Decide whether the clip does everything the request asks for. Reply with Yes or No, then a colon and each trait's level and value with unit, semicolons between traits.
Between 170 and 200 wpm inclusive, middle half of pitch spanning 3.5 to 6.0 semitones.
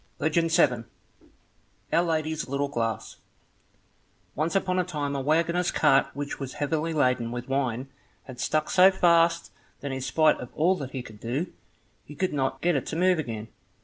Yes: average, 175 wpm; average, 4.0 semitones